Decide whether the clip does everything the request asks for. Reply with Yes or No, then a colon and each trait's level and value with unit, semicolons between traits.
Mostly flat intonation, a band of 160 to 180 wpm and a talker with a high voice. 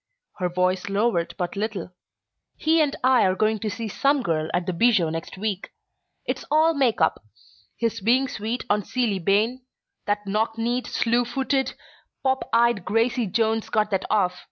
No: average, 4.1 semitones; average, 170 wpm; high, 220 Hz